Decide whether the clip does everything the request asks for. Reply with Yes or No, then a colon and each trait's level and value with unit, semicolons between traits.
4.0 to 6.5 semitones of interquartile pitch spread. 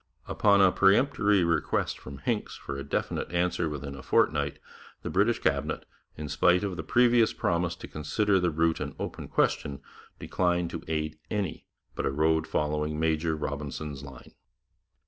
No: average, 3.6 semitones